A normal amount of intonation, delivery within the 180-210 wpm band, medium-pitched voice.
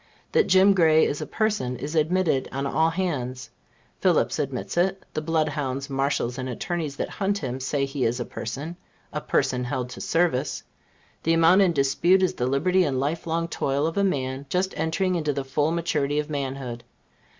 Yes: average, 4.2 semitones; average, 190 wpm; medium, 150 Hz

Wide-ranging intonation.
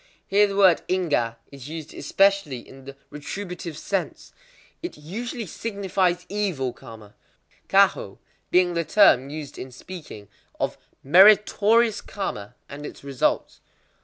Yes: wide, 6.4 semitones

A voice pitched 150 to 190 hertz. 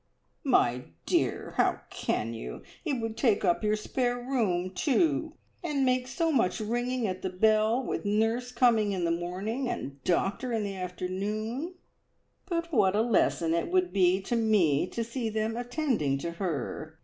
No: high, 220 Hz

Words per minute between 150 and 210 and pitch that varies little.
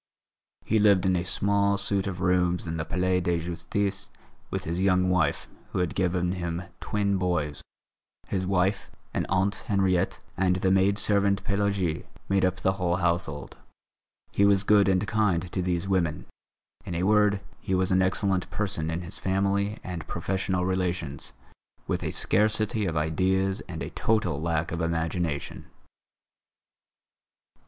Yes: average, 155 wpm; narrow, 2.3 semitones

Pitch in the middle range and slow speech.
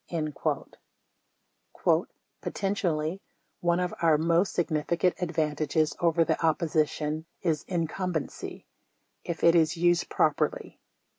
Yes: medium, 165 Hz; slow, 105 wpm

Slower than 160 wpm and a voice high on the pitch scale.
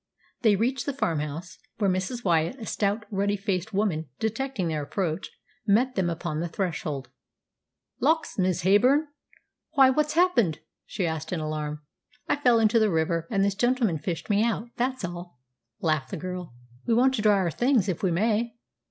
No: average, 175 wpm; high, 195 Hz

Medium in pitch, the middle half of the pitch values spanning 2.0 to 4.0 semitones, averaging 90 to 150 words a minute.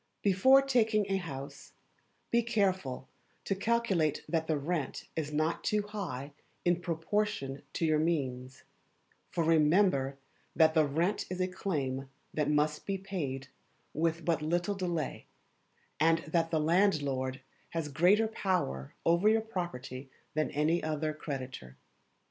No: medium, 165 Hz; average, 4.8 semitones; slow, 135 wpm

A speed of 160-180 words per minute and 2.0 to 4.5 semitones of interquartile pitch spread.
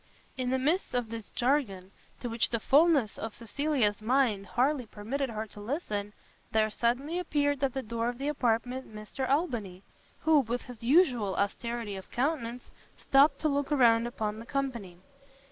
Yes: average, 170 wpm; average, 4.2 semitones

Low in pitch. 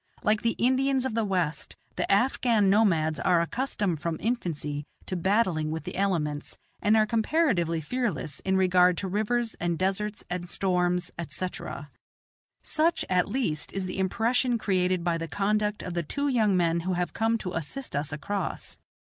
No: high, 190 Hz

